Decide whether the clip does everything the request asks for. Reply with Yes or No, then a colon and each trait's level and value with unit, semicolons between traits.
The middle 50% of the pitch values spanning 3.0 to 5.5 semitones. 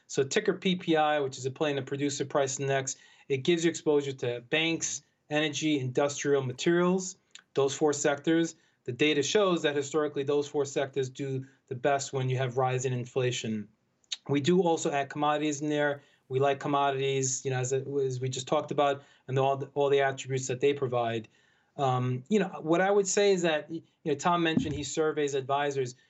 No: narrow, 2.4 semitones